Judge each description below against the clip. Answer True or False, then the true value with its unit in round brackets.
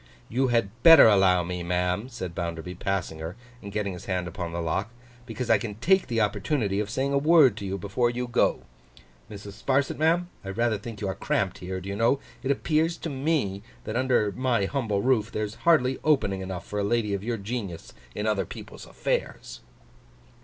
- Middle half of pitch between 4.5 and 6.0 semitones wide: True (4.9 semitones)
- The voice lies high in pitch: False (105 Hz)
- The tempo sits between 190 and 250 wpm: True (200 wpm)